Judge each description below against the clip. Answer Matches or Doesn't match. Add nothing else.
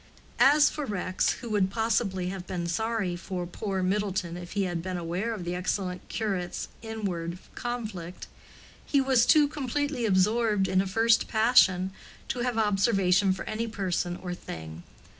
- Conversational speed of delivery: Matches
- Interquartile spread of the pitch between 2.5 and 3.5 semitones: Doesn't match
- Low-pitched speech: Doesn't match